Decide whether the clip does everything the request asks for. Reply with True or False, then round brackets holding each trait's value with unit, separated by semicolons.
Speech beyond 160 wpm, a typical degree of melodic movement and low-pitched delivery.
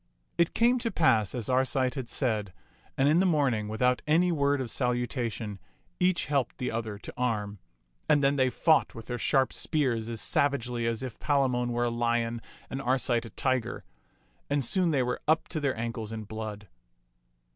True (185 wpm; 3.5 semitones; 125 Hz)